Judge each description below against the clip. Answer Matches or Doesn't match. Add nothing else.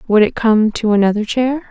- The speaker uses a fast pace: Matches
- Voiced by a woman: Matches